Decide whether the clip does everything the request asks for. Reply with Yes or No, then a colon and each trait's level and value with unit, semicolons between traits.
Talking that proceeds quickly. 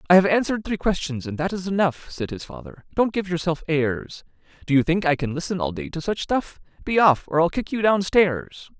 Yes: fast, 240 wpm